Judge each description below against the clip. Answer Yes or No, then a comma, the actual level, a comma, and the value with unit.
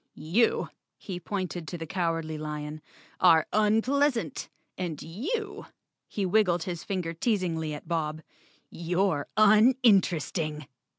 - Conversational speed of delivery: No, slow, 110 wpm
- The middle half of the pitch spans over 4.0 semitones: Yes, average, 4.7 semitones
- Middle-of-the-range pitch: Yes, medium, 175 Hz